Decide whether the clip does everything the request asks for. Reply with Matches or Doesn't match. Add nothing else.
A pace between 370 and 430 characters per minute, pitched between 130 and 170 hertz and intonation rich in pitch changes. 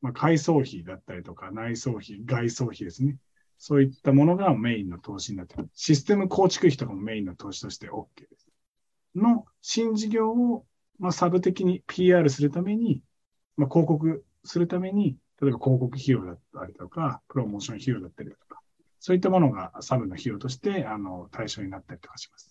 Matches